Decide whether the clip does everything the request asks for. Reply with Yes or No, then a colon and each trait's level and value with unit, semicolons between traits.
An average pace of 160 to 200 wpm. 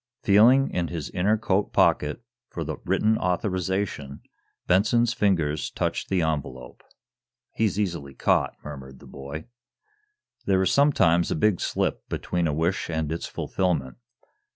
No: slow, 135 wpm